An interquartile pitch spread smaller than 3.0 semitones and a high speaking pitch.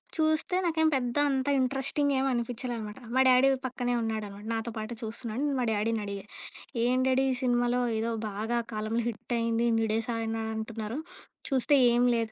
Yes: narrow, 2.6 semitones; high, 235 Hz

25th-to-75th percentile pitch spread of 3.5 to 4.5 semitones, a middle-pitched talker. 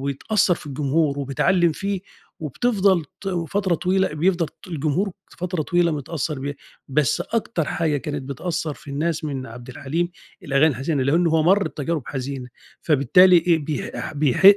Yes: average, 4.1 semitones; medium, 155 Hz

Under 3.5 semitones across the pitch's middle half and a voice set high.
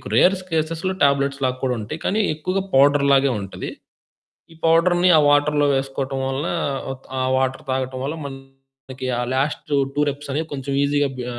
No: narrow, 2.6 semitones; medium, 140 Hz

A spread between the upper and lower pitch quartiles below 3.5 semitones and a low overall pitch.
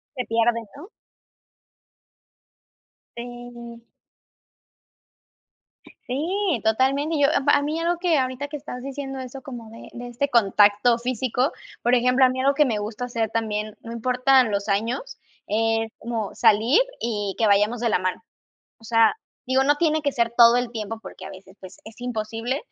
No: average, 3.1 semitones; high, 240 Hz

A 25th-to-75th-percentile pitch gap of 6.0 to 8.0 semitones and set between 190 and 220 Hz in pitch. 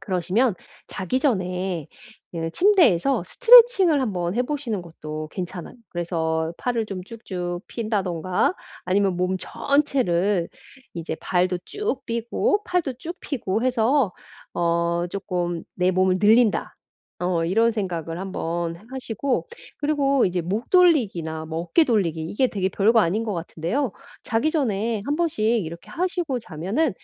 Yes: wide, 6.7 semitones; high, 200 Hz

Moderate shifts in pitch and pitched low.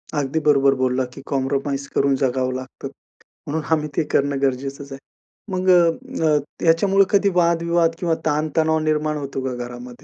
No: average, 3.3 semitones; medium, 150 Hz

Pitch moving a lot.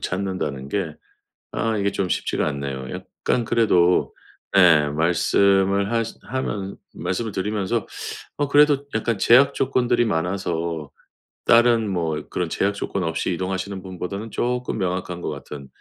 No: average, 4.6 semitones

